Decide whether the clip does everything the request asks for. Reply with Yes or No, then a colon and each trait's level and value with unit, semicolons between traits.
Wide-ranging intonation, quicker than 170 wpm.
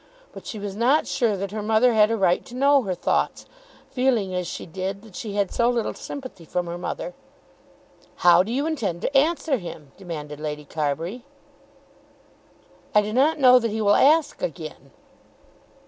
Yes: wide, 6.1 semitones; average, 180 wpm